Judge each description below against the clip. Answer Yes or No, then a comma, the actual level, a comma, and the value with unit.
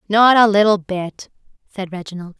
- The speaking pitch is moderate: No, high, 195 Hz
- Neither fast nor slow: Yes, average, 150 wpm